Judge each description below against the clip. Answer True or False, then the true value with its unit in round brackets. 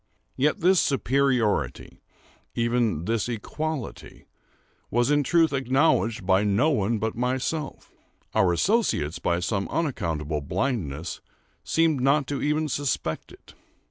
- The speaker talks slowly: True (110 wpm)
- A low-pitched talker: True (125 Hz)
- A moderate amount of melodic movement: False (6.6 semitones)